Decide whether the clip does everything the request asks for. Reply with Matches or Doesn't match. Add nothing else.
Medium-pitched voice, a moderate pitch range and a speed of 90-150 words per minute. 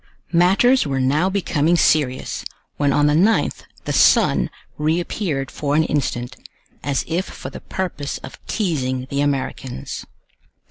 Matches